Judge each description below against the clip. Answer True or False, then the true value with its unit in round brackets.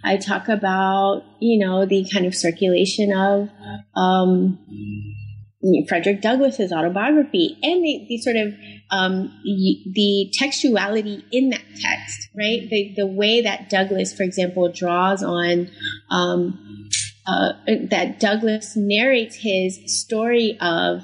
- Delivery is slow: True (125 wpm)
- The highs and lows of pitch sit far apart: False (3.7 semitones)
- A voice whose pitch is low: False (195 Hz)